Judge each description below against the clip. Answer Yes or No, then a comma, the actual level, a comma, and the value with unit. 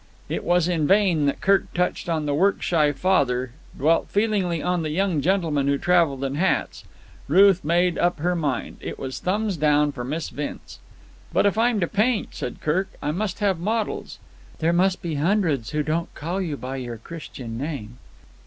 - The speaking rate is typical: Yes, average, 190 wpm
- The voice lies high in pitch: No, medium, 165 Hz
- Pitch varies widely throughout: No, average, 4.6 semitones